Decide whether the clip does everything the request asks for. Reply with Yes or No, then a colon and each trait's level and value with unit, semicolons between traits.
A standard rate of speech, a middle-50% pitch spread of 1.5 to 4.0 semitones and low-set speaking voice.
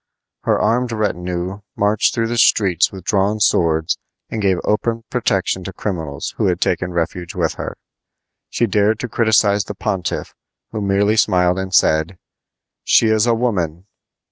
Yes: average, 155 wpm; average, 3.5 semitones; low, 100 Hz